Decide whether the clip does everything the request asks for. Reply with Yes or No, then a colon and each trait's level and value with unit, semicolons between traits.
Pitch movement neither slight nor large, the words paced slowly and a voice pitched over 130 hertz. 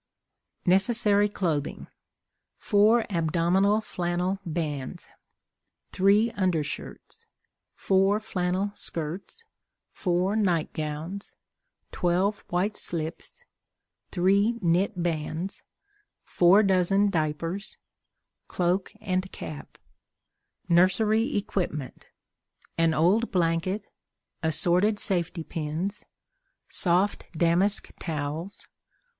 Yes: average, 3.3 semitones; slow, 75 wpm; medium, 185 Hz